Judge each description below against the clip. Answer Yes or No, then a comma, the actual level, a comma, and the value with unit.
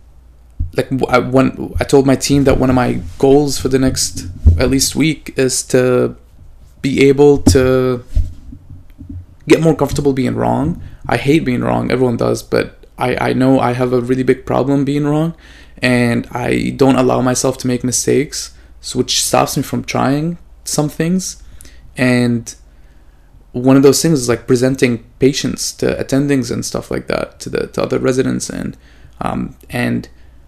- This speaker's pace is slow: No, average, 165 wpm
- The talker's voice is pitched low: Yes, low, 125 Hz